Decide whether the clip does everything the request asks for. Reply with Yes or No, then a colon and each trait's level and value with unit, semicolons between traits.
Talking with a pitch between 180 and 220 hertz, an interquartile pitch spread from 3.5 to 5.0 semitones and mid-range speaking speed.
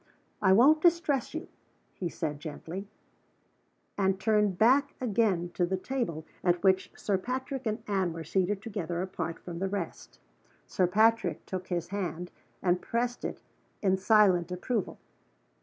Yes: high, 190 Hz; average, 4.3 semitones; average, 145 wpm